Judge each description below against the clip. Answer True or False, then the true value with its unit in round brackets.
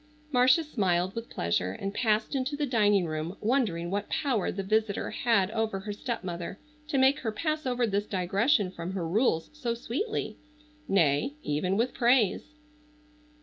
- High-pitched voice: True (215 Hz)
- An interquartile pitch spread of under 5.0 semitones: False (5.6 semitones)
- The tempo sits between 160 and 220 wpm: False (150 wpm)